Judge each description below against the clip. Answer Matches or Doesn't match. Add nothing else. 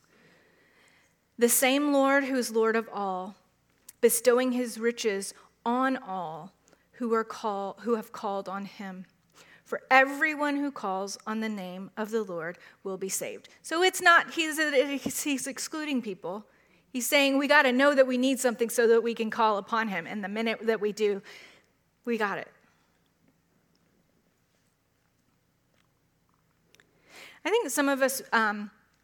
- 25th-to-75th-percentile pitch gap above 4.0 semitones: Matches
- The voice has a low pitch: Doesn't match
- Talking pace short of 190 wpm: Matches